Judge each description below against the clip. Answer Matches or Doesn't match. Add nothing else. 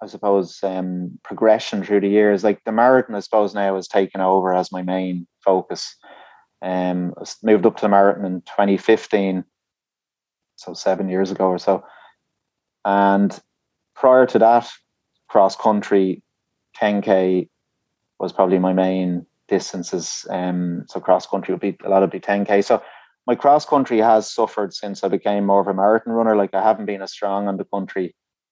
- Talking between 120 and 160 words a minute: Doesn't match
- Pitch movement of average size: Doesn't match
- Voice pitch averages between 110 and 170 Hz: Doesn't match